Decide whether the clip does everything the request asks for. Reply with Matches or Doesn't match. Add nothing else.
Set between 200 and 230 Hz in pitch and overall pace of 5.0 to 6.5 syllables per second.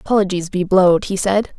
Doesn't match